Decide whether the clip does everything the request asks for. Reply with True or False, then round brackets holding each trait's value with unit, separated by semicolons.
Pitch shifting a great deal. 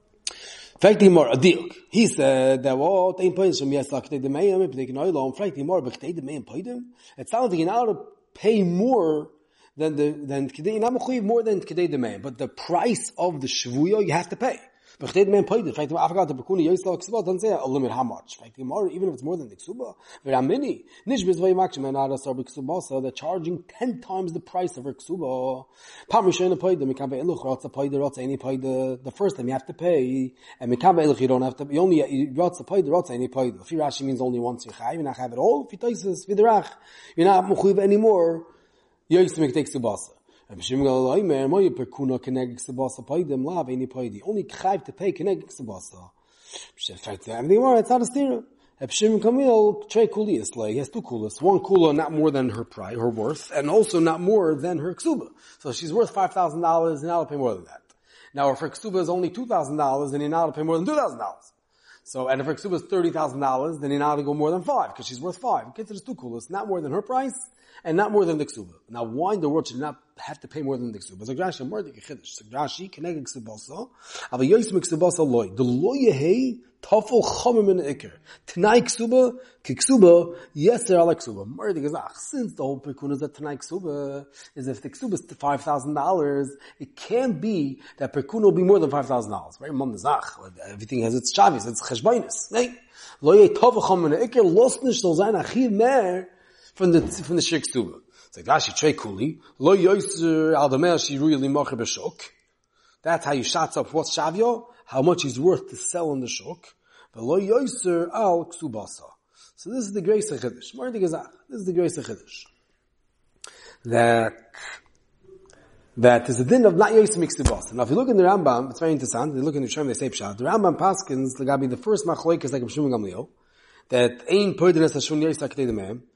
True (7.3 semitones)